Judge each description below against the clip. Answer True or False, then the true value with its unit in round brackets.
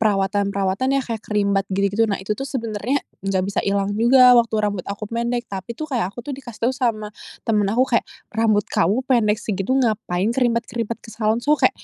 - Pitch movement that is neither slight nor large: True (3.0 semitones)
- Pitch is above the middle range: True (220 Hz)